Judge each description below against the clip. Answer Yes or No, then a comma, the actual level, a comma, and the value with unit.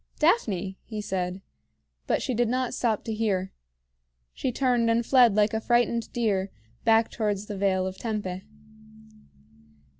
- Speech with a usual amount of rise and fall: Yes, average, 3.6 semitones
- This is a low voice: No, high, 220 Hz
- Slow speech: No, average, 145 wpm